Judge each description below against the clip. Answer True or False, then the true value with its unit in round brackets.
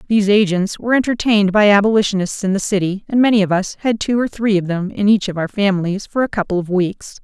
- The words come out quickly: True (240 wpm)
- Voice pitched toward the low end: False (200 Hz)